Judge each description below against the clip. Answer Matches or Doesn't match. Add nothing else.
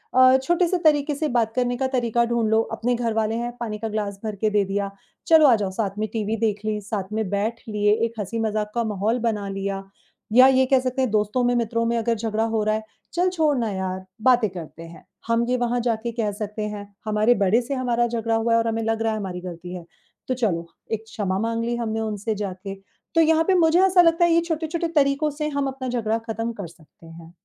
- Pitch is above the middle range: Matches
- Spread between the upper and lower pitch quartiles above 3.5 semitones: Doesn't match